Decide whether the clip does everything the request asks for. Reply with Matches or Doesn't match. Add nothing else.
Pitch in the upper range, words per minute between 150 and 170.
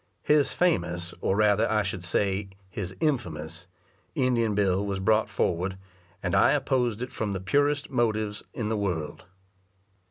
Doesn't match